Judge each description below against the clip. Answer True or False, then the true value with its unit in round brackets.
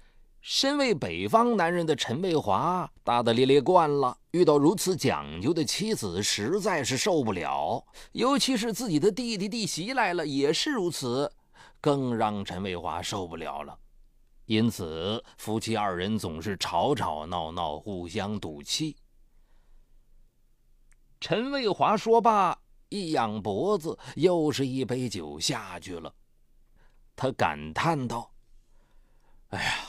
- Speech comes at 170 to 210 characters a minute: True (195 characters per minute)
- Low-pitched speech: True (130 Hz)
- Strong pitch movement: True (8.9 semitones)